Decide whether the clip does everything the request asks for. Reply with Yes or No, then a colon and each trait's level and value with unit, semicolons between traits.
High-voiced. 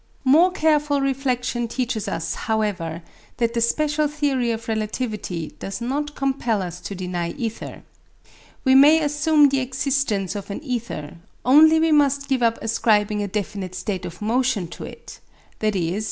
Yes: high, 235 Hz